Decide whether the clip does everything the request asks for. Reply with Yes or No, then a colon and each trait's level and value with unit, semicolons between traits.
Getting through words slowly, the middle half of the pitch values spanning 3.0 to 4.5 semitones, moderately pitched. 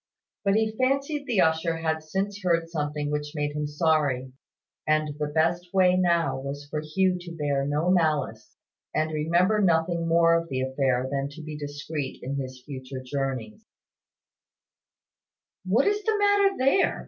No: average, 160 wpm; average, 4.0 semitones; medium, 160 Hz